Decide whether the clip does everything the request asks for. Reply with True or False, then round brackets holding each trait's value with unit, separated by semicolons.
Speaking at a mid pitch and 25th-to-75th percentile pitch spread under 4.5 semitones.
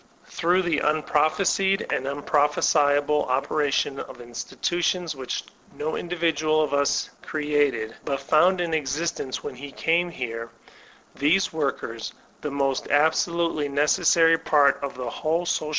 True (150 Hz; 2.9 semitones)